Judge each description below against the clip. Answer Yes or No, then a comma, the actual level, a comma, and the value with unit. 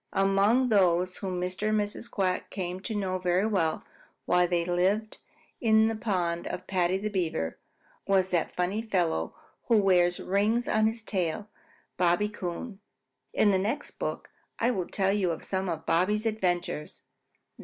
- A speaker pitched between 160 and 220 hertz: Yes, high, 190 Hz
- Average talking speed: Yes, average, 160 wpm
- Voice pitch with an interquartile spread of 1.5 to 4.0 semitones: Yes, average, 3.1 semitones